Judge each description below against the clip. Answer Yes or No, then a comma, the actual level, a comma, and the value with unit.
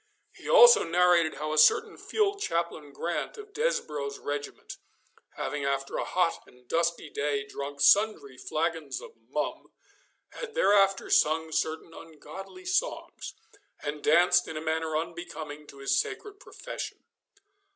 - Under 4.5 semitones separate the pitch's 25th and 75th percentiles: No, average, 4.9 semitones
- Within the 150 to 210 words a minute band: No, slow, 135 wpm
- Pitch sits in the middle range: Yes, medium, 160 Hz